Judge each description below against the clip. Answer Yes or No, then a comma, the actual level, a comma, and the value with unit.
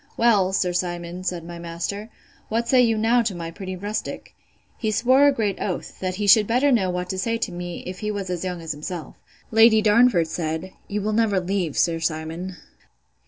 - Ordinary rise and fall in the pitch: Yes, average, 3.9 semitones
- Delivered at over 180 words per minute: Yes, average, 200 wpm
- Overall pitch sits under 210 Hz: Yes, high, 190 Hz